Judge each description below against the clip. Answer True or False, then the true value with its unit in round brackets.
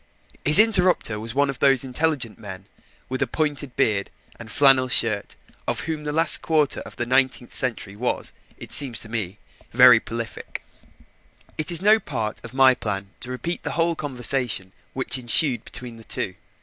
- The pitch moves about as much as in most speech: True (4.5 semitones)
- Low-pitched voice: True (130 Hz)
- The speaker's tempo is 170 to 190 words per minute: True (175 wpm)